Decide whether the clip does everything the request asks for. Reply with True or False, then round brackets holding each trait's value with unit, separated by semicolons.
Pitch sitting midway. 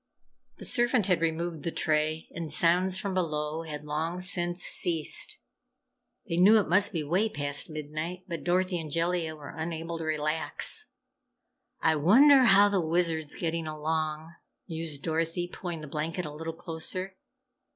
True (165 Hz)